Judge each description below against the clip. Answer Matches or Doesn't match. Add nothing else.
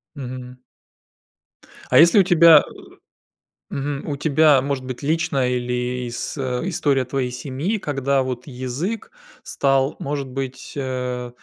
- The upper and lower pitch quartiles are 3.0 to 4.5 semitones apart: Doesn't match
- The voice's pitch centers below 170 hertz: Matches